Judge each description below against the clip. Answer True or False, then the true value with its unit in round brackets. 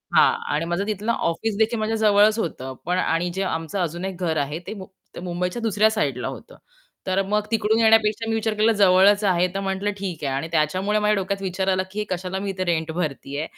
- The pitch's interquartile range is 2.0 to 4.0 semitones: True (3.5 semitones)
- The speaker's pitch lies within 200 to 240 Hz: False (190 Hz)